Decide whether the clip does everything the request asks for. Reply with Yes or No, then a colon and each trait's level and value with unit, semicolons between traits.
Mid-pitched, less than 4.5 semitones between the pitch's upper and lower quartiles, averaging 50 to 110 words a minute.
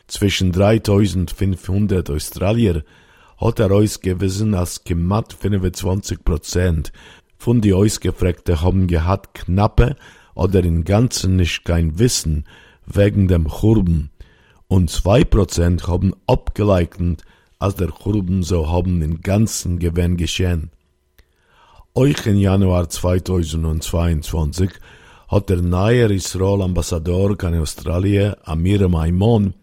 No: very low, 90 Hz; average, 2.9 semitones; slow, 100 wpm